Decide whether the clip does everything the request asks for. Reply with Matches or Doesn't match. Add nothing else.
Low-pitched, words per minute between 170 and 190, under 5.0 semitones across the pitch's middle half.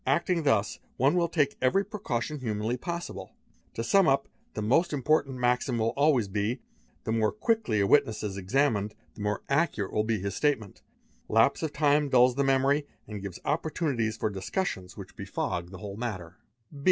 Doesn't match